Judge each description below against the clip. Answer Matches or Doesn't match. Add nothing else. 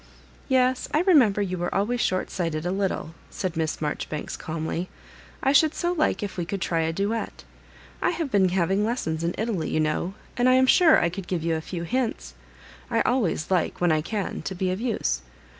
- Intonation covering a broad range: Matches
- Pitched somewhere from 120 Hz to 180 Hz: Doesn't match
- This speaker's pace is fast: Matches